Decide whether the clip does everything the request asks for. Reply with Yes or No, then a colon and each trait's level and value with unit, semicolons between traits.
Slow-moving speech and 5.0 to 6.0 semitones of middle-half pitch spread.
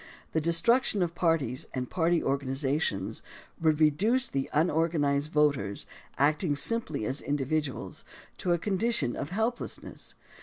No: slow, 125 wpm; average, 3.8 semitones